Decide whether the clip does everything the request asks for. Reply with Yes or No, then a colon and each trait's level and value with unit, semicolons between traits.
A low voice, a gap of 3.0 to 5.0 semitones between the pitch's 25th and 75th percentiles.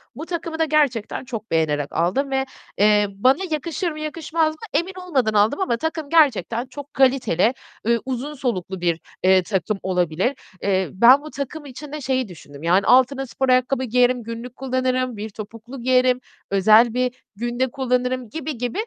No: very high, 250 Hz; average, 4.6 semitones